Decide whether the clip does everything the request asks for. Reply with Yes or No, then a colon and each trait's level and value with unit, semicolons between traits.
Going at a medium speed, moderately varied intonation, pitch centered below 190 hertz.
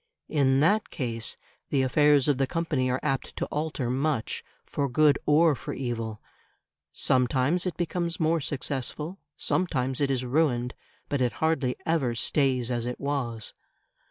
Yes: average, 150 wpm; average, 3.7 semitones; low, 135 Hz